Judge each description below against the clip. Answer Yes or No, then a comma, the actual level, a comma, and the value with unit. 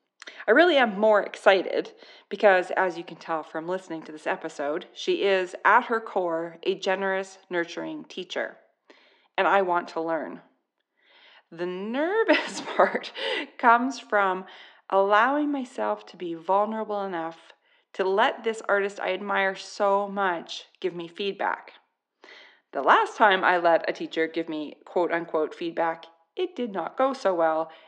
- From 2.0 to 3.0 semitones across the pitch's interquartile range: No, average, 4.6 semitones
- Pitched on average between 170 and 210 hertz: Yes, high, 190 Hz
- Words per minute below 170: Yes, average, 150 wpm